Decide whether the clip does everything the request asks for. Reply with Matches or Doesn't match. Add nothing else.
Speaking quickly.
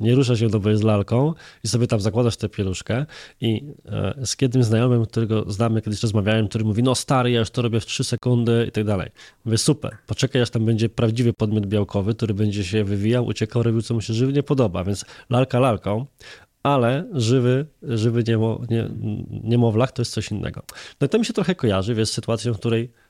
Matches